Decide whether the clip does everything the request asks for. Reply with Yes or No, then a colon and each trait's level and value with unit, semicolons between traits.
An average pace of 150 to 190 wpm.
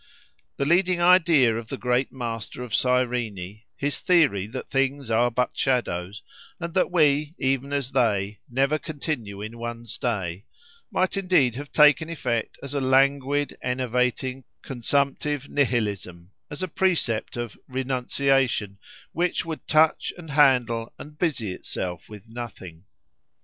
No: slow, 135 wpm